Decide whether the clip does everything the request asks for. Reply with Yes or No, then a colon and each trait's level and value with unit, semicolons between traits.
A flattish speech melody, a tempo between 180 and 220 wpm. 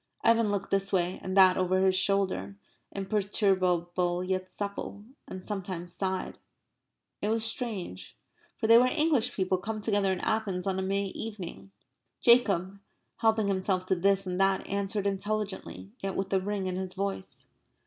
No: narrow, 1.7 semitones; average, 160 wpm